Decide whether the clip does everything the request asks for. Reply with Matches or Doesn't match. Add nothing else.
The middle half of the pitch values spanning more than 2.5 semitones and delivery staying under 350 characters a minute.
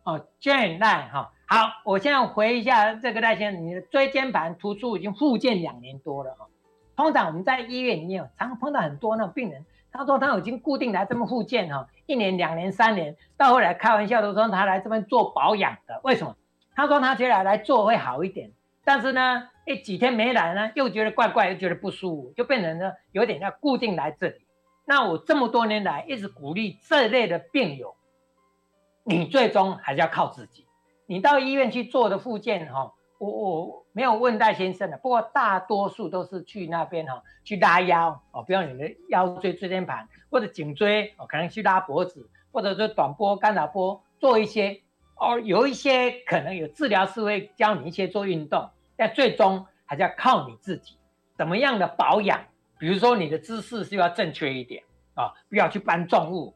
Matches